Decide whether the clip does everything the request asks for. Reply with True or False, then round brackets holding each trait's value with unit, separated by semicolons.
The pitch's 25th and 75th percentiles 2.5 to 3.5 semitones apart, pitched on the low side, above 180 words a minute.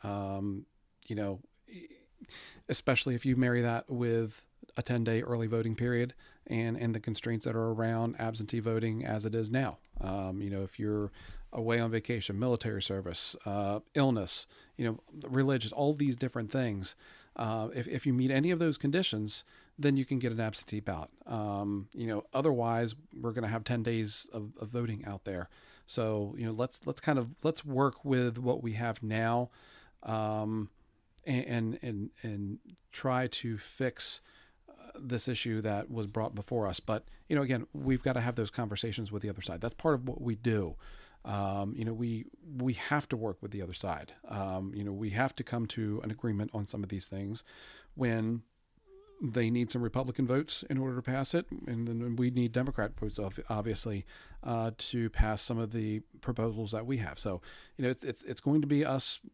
True (3.0 semitones; 115 Hz; 190 wpm)